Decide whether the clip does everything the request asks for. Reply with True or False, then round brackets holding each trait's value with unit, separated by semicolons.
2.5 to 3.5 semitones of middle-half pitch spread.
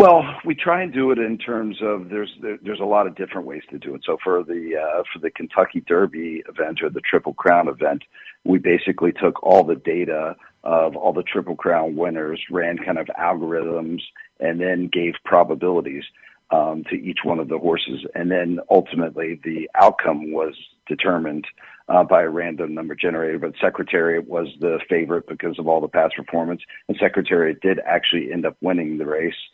False (4.1 semitones)